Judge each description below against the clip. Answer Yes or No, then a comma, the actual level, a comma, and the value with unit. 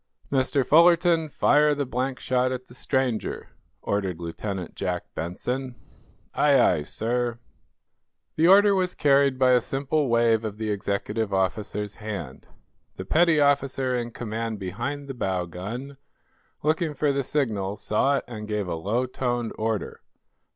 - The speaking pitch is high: No, low, 125 Hz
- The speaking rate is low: No, average, 145 wpm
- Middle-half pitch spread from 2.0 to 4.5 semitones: No, average, 5.0 semitones